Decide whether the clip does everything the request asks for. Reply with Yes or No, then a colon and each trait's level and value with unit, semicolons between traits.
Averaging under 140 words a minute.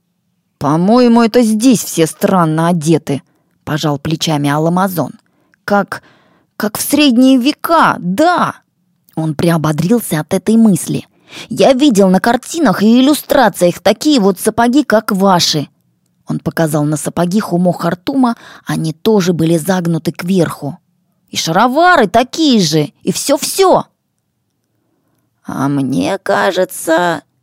Yes: slow, 110 wpm